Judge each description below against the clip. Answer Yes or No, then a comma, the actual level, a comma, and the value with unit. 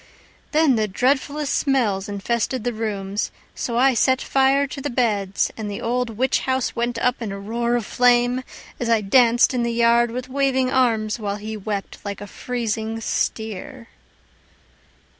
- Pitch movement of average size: Yes, average, 3.0 semitones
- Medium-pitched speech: No, high, 235 Hz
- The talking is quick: No, average, 165 wpm